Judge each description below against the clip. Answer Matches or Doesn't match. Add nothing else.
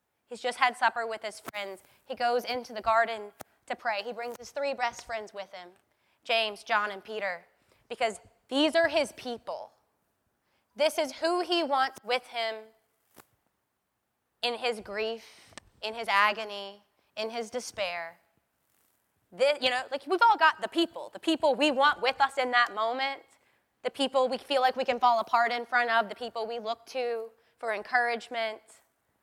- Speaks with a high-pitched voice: Matches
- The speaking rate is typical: Matches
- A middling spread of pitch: Matches